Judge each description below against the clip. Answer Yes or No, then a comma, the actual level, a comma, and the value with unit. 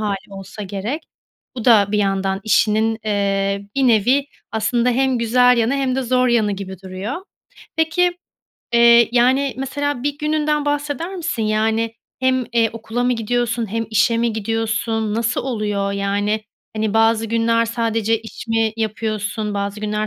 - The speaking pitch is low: No, high, 225 Hz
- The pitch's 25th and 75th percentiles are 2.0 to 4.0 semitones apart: Yes, average, 2.9 semitones